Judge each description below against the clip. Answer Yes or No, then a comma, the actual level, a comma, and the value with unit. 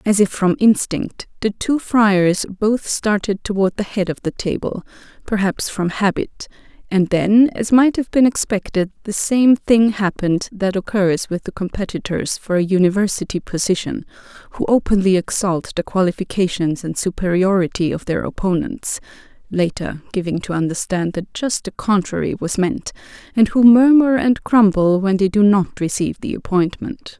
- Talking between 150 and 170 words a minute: Yes, average, 155 wpm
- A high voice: Yes, high, 200 Hz